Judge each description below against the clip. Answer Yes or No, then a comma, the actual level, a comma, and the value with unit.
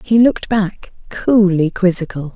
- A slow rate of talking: Yes, slow, 130 wpm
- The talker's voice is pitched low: No, high, 190 Hz